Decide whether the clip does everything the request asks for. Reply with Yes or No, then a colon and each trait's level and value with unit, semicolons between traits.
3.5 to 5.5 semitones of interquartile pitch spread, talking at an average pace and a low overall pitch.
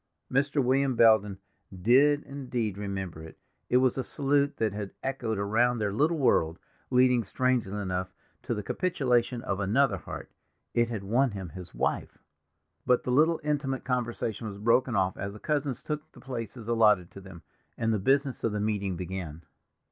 Yes: average, 5.0 semitones; average, 170 wpm; low, 115 Hz